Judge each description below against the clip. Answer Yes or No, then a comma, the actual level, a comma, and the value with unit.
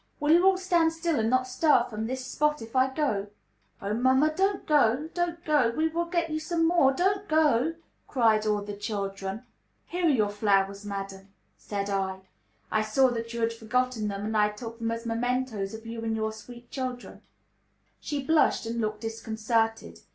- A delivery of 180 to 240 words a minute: Yes, average, 190 wpm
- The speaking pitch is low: No, high, 235 Hz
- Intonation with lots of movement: Yes, wide, 5.8 semitones